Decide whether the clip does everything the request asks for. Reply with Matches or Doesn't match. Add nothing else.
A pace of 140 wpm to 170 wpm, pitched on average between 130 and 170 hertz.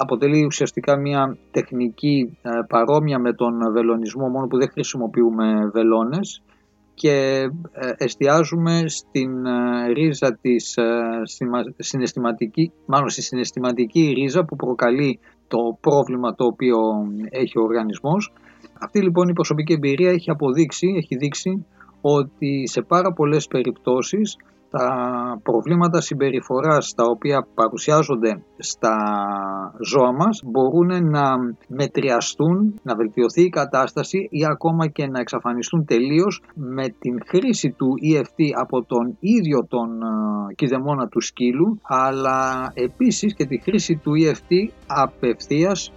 Doesn't match